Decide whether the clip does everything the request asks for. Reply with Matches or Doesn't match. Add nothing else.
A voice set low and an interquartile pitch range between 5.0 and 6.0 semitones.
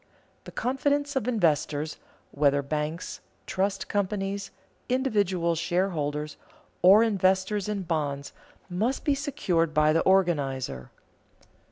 Doesn't match